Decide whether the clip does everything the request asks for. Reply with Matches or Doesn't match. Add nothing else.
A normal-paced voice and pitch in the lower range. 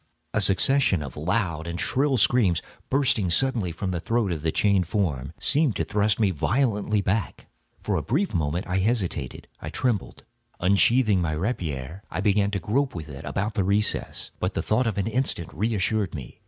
Matches